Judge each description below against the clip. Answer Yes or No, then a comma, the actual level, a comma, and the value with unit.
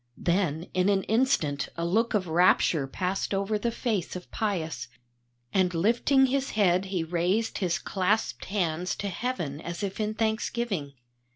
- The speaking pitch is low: No, high, 190 Hz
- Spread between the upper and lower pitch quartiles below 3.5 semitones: No, average, 4.2 semitones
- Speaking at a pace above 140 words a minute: Yes, average, 155 wpm